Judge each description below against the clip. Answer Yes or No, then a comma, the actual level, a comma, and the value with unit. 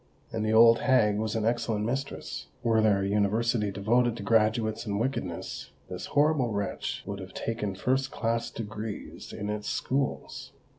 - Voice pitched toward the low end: Yes, low, 110 Hz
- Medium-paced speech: Yes, average, 160 wpm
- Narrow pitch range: Yes, narrow, 2.2 semitones